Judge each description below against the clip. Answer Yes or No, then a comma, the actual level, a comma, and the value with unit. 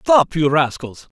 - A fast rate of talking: No, average, 150 wpm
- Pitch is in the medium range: Yes, medium, 160 Hz